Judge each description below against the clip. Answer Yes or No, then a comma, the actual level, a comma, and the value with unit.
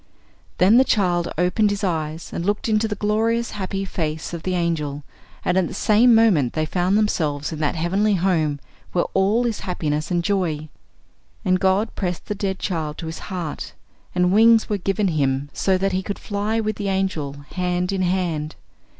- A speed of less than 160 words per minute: No, average, 185 wpm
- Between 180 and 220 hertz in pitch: Yes, medium, 185 Hz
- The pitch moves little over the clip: No, average, 4.0 semitones